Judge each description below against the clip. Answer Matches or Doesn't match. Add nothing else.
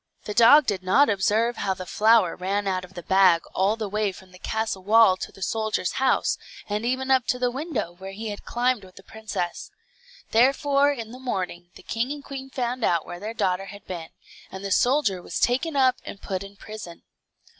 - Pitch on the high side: Matches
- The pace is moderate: Doesn't match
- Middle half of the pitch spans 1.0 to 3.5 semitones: Doesn't match